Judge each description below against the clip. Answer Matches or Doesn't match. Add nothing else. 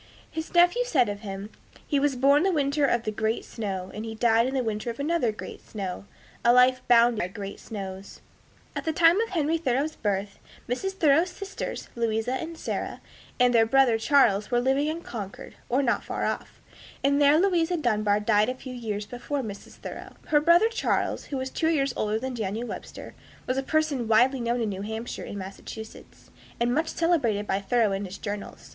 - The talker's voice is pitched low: Doesn't match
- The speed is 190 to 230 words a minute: Matches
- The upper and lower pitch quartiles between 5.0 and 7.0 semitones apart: Matches